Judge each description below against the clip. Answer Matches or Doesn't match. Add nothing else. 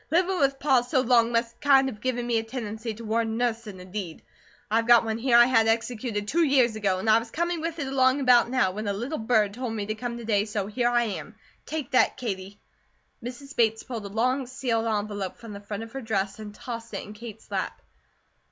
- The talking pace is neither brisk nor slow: Doesn't match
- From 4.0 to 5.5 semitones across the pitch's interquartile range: Doesn't match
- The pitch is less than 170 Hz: Doesn't match